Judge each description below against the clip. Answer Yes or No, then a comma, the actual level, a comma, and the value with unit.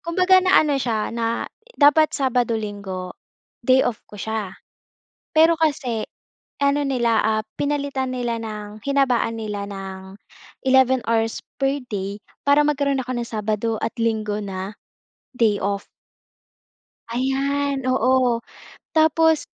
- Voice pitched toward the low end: No, high, 240 Hz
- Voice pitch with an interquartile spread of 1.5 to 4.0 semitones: No, average, 4.7 semitones